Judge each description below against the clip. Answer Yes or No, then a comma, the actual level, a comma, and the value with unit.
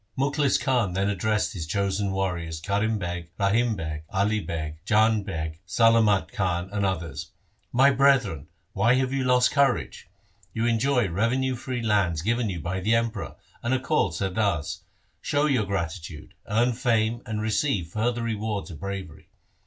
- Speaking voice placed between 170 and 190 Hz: No, low, 105 Hz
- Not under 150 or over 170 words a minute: Yes, average, 160 wpm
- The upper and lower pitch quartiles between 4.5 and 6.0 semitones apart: Yes, average, 4.8 semitones